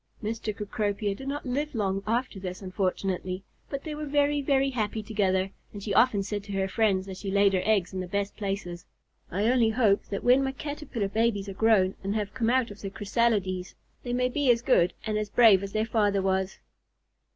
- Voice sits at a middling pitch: No, high, 210 Hz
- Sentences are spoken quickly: Yes, fast, 210 wpm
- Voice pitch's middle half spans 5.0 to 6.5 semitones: No, average, 3.8 semitones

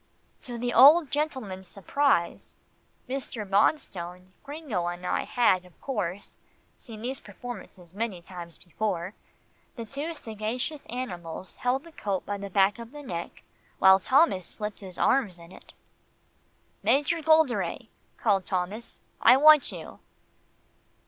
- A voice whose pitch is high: Yes, high, 215 Hz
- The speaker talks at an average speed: No, slow, 130 wpm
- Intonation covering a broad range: Yes, wide, 6.4 semitones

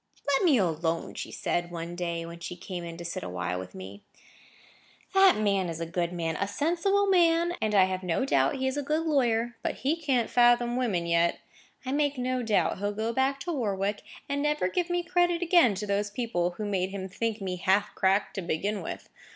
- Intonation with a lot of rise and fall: Yes, wide, 7.7 semitones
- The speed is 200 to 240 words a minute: Yes, fast, 205 wpm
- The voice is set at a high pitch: Yes, high, 205 Hz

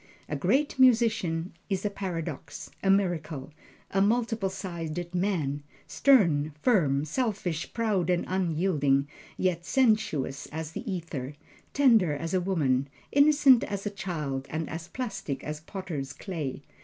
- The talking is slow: Yes, slow, 130 wpm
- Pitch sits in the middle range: Yes, medium, 175 Hz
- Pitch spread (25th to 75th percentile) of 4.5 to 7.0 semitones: Yes, average, 5.3 semitones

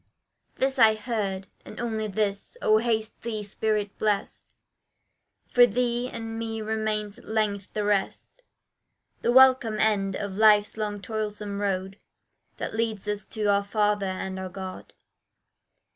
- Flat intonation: Yes, narrow, 1.6 semitones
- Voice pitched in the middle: No, high, 215 Hz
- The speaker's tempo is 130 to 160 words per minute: Yes, average, 140 wpm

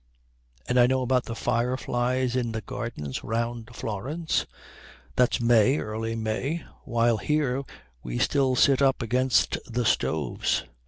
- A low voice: Yes, low, 120 Hz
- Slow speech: Yes, slow, 130 wpm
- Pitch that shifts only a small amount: Yes, narrow, 2.3 semitones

